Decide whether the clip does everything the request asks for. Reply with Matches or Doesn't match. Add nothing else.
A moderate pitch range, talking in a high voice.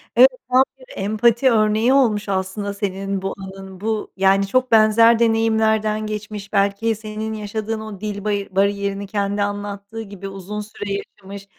Doesn't match